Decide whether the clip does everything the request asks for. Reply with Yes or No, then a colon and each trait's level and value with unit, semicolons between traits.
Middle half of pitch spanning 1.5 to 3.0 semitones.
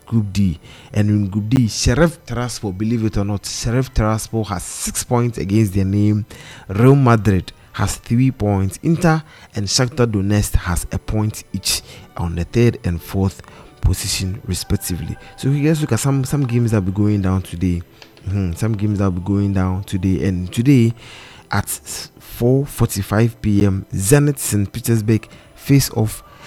No: average, 3.7 semitones